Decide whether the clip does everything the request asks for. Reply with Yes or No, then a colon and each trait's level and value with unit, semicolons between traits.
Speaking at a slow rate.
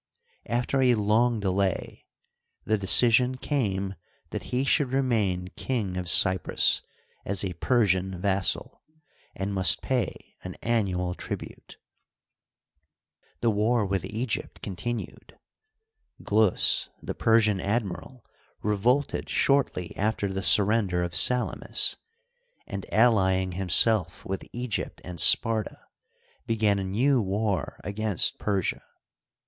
Yes: slow, 110 wpm